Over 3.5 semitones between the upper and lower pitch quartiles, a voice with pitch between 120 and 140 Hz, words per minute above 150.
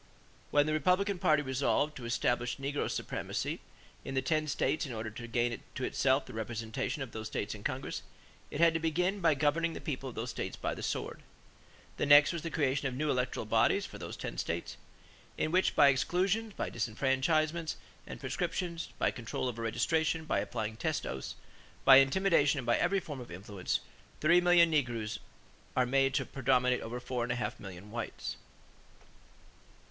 Yes: average, 4.9 semitones; low, 135 Hz; average, 185 wpm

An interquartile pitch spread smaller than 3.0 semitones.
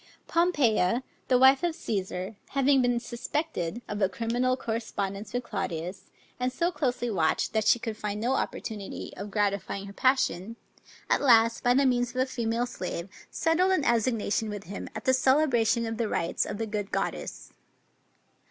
No: average, 3.9 semitones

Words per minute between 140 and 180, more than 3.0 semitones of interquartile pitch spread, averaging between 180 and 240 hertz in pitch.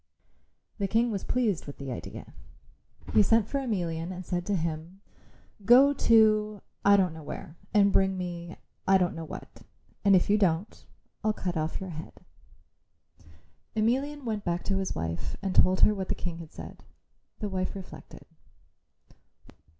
Yes: average, 165 wpm; average, 3.7 semitones; high, 190 Hz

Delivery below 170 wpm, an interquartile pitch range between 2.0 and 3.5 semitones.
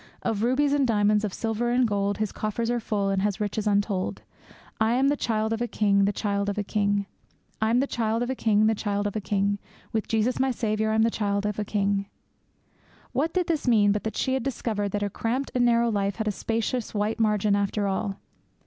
No: average, 190 wpm; narrow, 2.4 semitones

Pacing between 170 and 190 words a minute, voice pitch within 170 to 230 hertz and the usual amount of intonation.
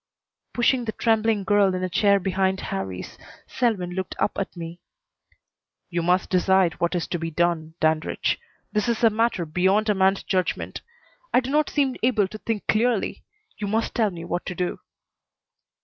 Yes: average, 175 wpm; high, 190 Hz; average, 4.0 semitones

